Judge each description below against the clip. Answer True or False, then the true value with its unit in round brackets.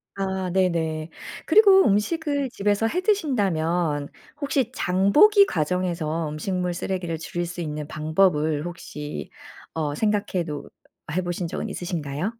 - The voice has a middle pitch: True (180 Hz)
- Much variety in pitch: False (4.6 semitones)